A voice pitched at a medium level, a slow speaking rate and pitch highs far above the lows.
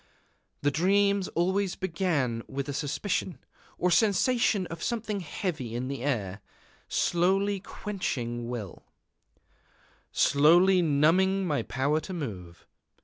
Yes: medium, 165 Hz; slow, 110 wpm; wide, 6.0 semitones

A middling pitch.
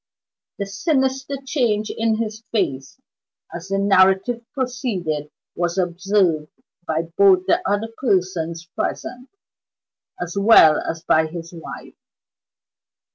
No: high, 195 Hz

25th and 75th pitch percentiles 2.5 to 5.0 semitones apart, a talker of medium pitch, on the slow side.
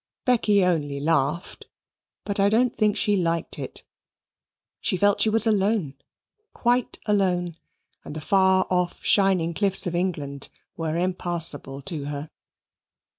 Yes: average, 4.0 semitones; medium, 180 Hz; slow, 130 wpm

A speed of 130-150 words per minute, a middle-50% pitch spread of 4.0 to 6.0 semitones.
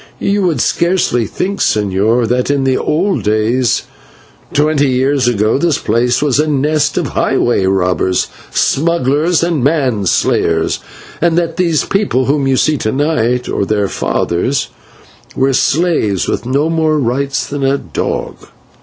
Yes: average, 145 wpm; average, 4.7 semitones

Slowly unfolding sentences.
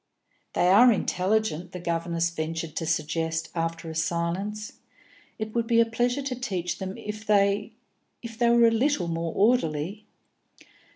No: average, 155 wpm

